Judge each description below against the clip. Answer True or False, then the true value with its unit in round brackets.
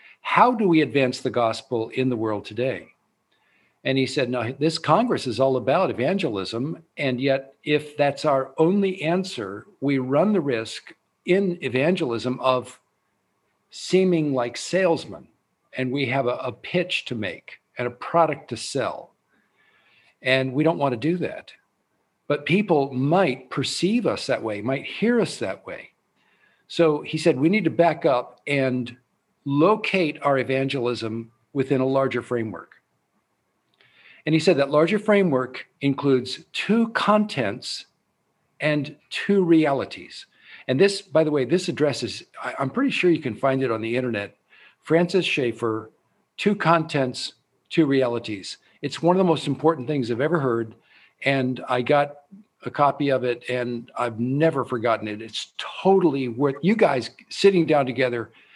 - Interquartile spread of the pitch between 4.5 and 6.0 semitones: True (5.0 semitones)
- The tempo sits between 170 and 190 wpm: False (155 wpm)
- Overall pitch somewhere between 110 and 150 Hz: True (140 Hz)